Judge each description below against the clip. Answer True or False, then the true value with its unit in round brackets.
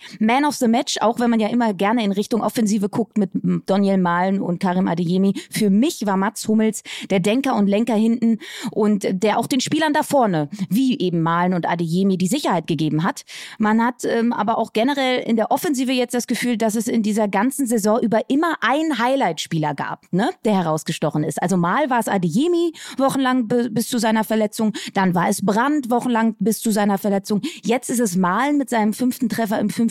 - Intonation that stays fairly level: False (3.7 semitones)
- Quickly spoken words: True (205 wpm)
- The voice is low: False (220 Hz)